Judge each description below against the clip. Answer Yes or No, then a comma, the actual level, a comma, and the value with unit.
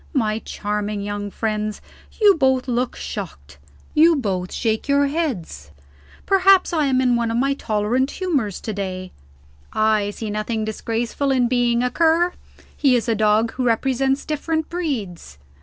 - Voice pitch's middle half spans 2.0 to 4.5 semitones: No, average, 4.9 semitones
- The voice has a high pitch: Yes, high, 235 Hz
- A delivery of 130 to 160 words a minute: Yes, average, 155 wpm